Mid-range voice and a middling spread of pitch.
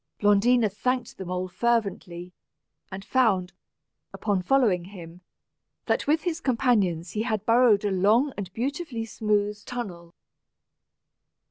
No: high, 210 Hz; average, 4.7 semitones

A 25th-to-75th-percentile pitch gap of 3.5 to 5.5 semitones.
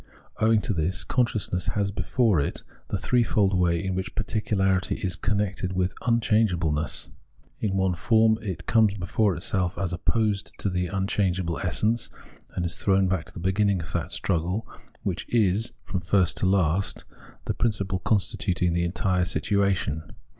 No: average, 2.8 semitones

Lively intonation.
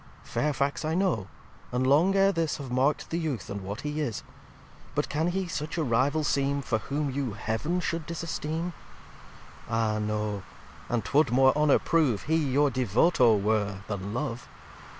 Yes: wide, 5.7 semitones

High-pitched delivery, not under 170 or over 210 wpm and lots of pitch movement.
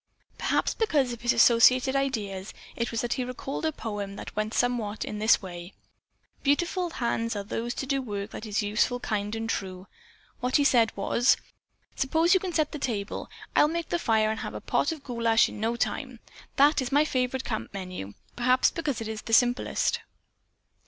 No: high, 235 Hz; average, 185 wpm; average, 4.0 semitones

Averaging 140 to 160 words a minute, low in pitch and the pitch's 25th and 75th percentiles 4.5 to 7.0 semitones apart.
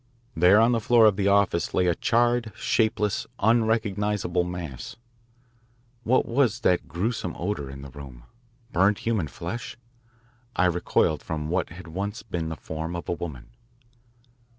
Yes: average, 150 wpm; very low, 95 Hz; average, 4.9 semitones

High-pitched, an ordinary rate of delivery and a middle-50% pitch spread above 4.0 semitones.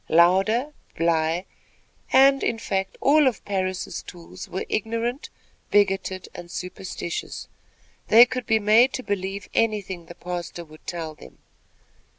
No: high, 195 Hz; slow, 130 wpm; average, 4.6 semitones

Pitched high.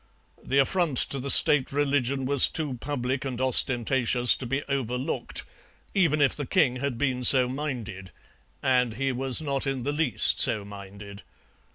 No: low, 130 Hz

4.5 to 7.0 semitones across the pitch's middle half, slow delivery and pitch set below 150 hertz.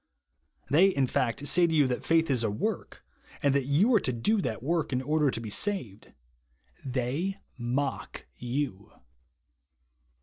No: average, 4.9 semitones; average, 160 wpm; medium, 140 Hz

